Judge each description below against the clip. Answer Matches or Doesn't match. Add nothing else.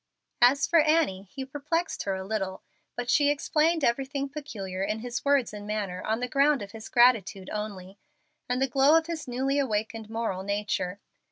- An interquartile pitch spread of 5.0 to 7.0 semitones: Matches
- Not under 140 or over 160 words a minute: Doesn't match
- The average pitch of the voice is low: Doesn't match